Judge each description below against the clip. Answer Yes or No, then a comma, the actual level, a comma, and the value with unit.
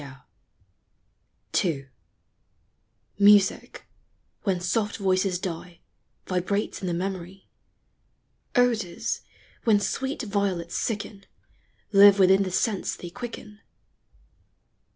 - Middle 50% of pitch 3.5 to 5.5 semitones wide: No, average, 2.7 semitones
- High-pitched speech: Yes, high, 195 Hz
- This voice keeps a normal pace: No, slow, 90 wpm